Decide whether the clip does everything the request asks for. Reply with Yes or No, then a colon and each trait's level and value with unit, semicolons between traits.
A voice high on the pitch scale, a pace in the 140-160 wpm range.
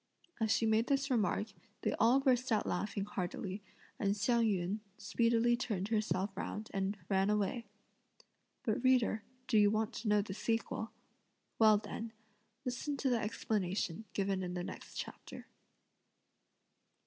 Yes: high, 215 Hz; average, 145 wpm